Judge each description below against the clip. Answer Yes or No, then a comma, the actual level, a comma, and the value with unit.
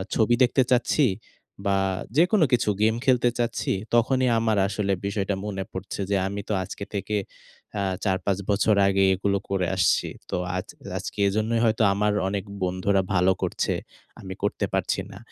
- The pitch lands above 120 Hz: No, low, 100 Hz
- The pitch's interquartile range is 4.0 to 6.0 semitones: No, average, 2.7 semitones